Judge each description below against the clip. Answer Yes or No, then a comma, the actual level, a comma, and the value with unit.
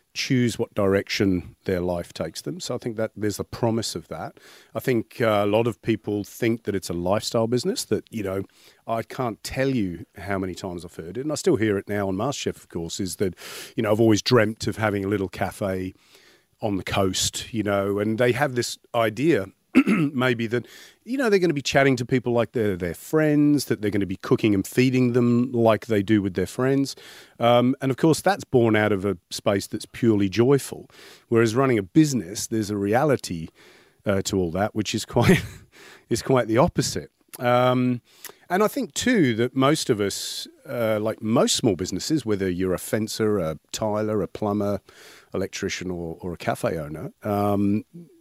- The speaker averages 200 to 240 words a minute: Yes, fast, 205 wpm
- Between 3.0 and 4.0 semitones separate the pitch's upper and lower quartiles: Yes, average, 3.7 semitones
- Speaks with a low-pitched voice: Yes, low, 110 Hz